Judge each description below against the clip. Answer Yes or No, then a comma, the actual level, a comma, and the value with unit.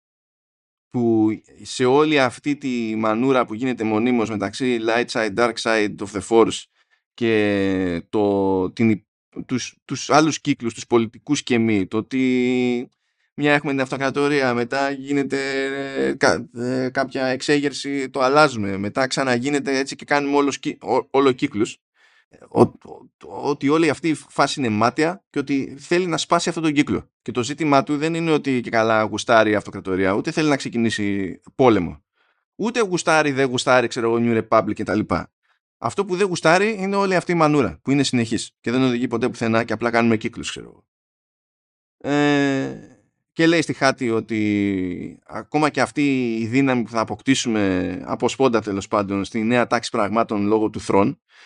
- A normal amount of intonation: Yes, average, 4.4 semitones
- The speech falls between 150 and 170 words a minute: Yes, average, 165 wpm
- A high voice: No, low, 125 Hz